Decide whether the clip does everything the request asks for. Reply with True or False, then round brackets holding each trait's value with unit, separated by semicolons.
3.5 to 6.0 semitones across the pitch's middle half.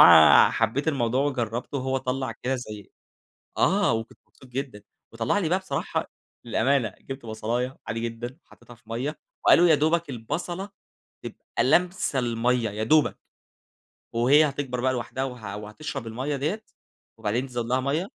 True (3.9 semitones)